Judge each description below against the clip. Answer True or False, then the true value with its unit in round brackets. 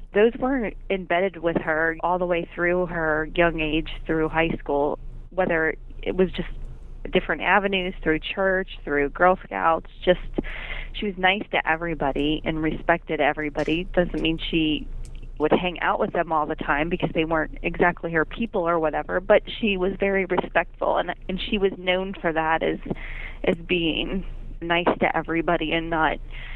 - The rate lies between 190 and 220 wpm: False (165 wpm)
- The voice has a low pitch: False (170 Hz)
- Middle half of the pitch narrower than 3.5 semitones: True (2.7 semitones)